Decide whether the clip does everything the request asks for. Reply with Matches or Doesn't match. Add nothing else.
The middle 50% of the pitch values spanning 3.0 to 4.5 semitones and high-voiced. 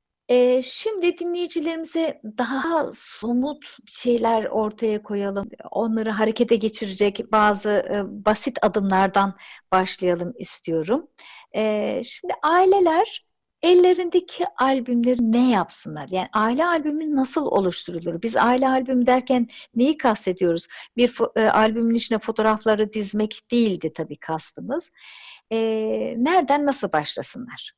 Doesn't match